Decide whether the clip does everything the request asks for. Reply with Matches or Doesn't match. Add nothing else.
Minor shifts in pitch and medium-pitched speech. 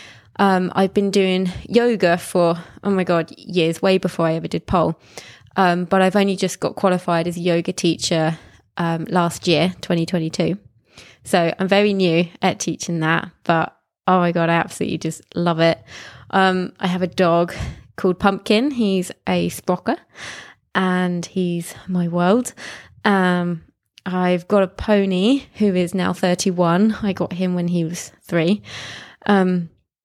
Matches